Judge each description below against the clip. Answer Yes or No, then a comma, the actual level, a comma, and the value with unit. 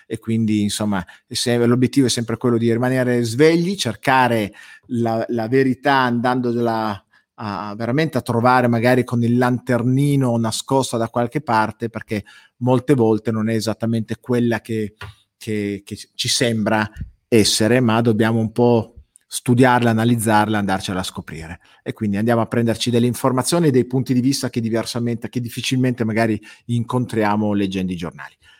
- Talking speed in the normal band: Yes, average, 145 wpm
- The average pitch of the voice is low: Yes, low, 115 Hz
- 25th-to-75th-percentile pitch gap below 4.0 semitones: Yes, narrow, 2.4 semitones